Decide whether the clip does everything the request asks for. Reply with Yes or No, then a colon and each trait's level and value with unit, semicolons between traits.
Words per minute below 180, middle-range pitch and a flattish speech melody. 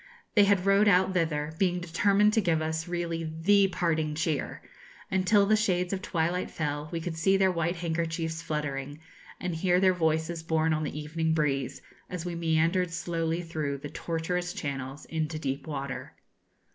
Yes: average, 170 wpm; medium, 165 Hz; narrow, 2.3 semitones